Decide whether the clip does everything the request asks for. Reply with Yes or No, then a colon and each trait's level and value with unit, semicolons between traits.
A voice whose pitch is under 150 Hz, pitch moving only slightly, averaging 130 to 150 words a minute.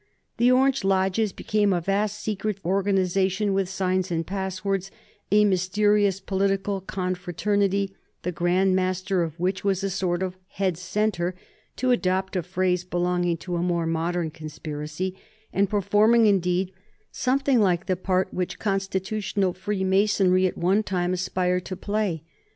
No: high, 190 Hz; narrow, 1.9 semitones; average, 140 wpm